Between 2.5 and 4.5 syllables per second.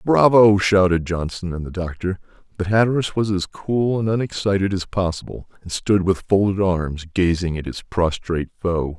No: 4.9 syllables/s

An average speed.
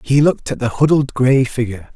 No: fast, 215 wpm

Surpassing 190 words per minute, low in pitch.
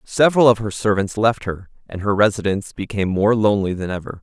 Yes: average, 200 wpm; low, 105 Hz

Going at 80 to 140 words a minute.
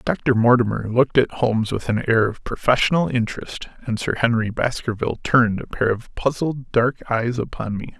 No: average, 180 wpm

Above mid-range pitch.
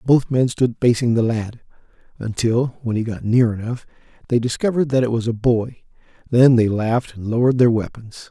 No: low, 120 Hz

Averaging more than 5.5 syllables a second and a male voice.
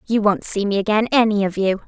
No: 6.1 syllables/s; female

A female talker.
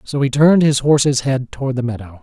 No: male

